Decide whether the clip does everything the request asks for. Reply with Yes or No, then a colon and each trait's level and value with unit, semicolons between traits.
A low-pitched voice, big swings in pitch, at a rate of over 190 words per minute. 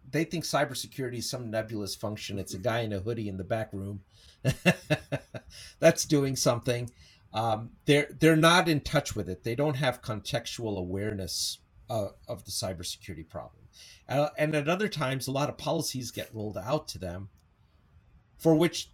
No: low, 115 Hz; wide, 6.5 semitones; average, 170 wpm